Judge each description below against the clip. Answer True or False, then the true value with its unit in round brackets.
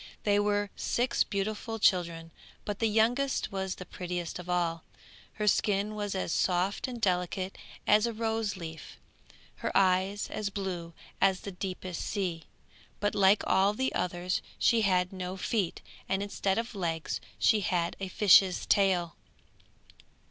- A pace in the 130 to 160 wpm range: True (145 wpm)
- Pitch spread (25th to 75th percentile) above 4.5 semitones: False (2.6 semitones)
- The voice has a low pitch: False (195 Hz)